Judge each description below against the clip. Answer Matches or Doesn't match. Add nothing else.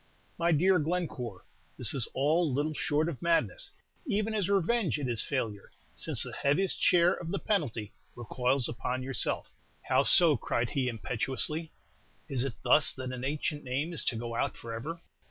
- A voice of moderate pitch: Matches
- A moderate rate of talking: Matches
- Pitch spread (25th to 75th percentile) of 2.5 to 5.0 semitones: Doesn't match